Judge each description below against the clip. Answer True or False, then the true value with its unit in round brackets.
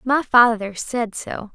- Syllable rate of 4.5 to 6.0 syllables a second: False (3.5 syllables/s)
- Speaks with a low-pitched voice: False (230 Hz)